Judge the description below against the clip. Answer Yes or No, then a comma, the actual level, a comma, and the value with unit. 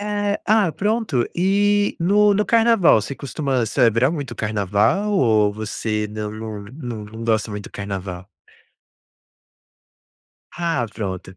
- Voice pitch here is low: Yes, low, 120 Hz